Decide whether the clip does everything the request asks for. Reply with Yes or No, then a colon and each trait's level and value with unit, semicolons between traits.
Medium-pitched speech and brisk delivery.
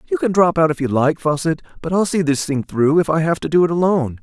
Yes: medium, 155 Hz; fast, 300 wpm